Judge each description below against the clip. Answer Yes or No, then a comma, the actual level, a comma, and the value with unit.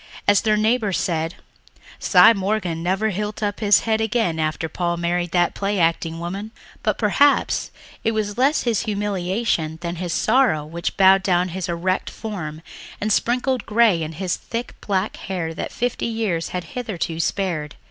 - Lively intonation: No, average, 4.2 semitones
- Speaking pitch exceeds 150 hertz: Yes, high, 190 Hz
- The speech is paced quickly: No, average, 165 wpm